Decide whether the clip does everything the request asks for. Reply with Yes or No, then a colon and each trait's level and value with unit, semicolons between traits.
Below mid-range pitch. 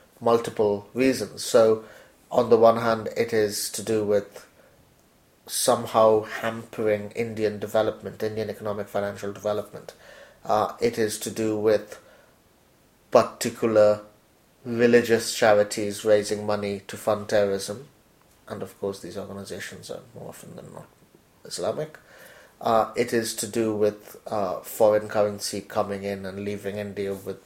Yes: low, 105 Hz